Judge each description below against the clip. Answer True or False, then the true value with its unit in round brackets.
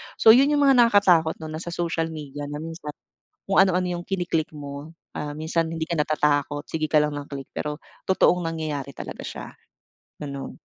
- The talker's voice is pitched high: False (160 Hz)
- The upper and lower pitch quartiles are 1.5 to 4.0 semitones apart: True (2.9 semitones)